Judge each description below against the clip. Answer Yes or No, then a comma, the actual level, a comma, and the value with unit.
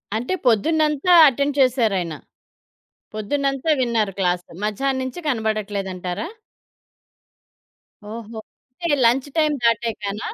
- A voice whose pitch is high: Yes, high, 235 Hz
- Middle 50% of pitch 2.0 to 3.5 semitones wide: No, average, 4.8 semitones